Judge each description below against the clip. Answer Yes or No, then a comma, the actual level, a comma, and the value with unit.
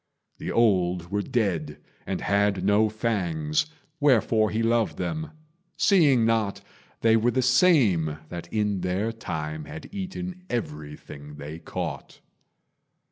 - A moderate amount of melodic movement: No, wide, 5.8 semitones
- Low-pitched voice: Yes, low, 105 Hz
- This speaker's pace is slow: Yes, slow, 125 wpm